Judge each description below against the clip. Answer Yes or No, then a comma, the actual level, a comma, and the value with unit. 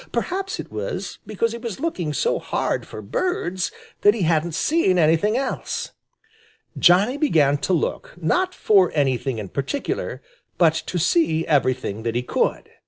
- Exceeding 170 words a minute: No, average, 155 wpm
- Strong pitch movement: Yes, wide, 7.5 semitones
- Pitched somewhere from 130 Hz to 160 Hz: No, medium, 175 Hz